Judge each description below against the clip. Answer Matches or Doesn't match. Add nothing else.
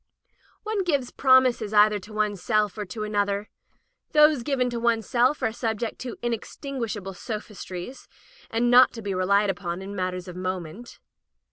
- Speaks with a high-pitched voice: Matches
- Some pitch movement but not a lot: Matches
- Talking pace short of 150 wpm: Doesn't match